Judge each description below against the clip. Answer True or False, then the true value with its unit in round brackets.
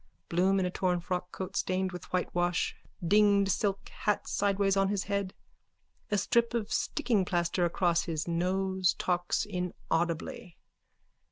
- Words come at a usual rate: False (125 wpm)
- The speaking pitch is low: False (185 Hz)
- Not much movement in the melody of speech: True (2.1 semitones)